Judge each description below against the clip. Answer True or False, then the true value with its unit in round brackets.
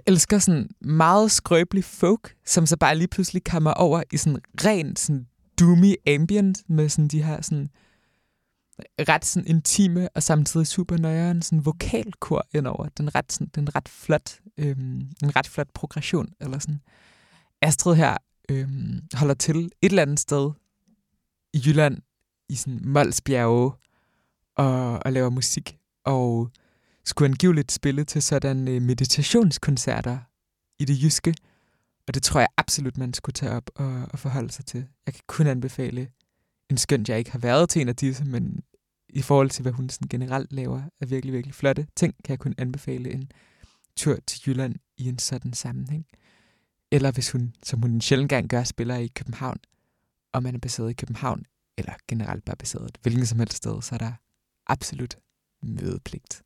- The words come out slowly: False (165 wpm)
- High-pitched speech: False (140 Hz)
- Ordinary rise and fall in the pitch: True (3.8 semitones)